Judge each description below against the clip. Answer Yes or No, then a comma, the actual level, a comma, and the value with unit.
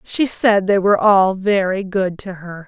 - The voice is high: Yes, high, 195 Hz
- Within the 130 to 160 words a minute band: No, average, 200 wpm